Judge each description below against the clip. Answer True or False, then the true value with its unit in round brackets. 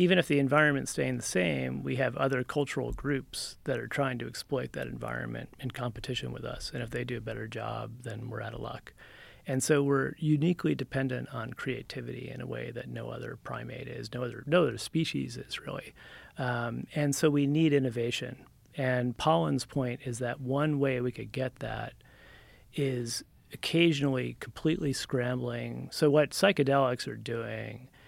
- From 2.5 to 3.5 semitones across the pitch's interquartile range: True (3.2 semitones)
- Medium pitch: False (130 Hz)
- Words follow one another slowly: False (175 wpm)